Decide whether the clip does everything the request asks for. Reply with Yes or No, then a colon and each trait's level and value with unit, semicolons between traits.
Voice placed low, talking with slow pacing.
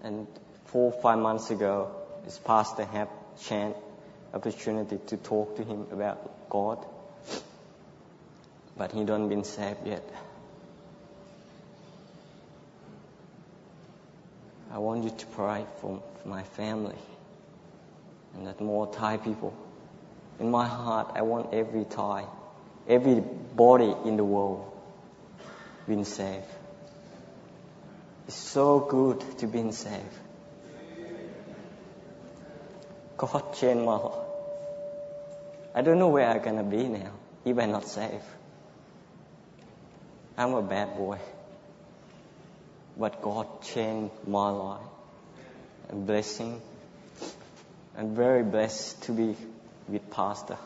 Yes: low, 110 Hz; slow, 110 wpm